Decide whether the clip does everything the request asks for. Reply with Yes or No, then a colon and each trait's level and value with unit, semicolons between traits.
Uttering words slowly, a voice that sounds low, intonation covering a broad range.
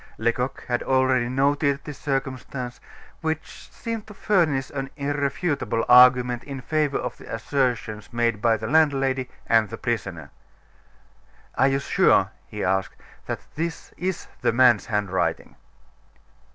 No: slow, 130 wpm; low, 130 Hz; average, 3.4 semitones